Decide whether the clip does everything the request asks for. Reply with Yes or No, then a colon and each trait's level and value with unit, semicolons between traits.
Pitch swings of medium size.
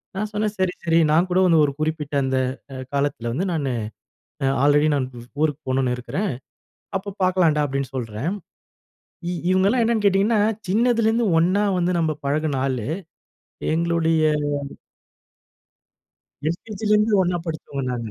No: wide, 5.7 semitones